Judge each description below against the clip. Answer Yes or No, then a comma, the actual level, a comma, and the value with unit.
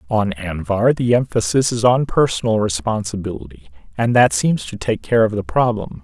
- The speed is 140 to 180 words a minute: Yes, average, 170 wpm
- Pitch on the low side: Yes, low, 105 Hz